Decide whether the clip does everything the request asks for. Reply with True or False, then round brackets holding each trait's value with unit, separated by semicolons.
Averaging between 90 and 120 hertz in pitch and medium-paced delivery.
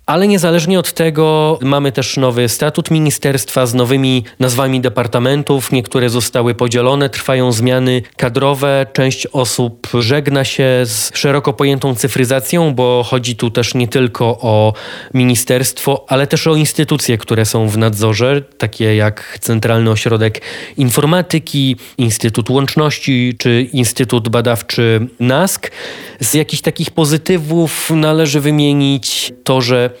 False (130 Hz; 125 wpm)